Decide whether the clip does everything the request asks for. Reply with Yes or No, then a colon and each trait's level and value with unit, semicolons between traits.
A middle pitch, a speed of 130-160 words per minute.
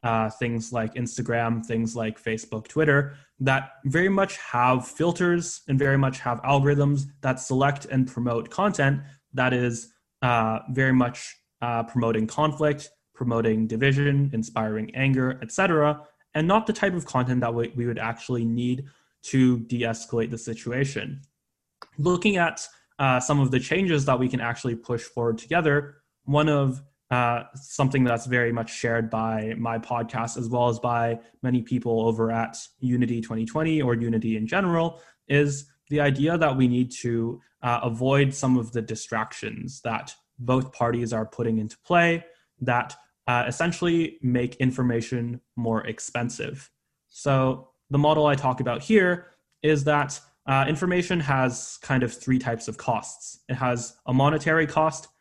No: low, 130 Hz; average, 155 wpm